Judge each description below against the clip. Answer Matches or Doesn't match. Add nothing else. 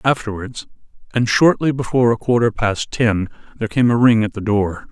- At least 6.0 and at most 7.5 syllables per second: Doesn't match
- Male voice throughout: Matches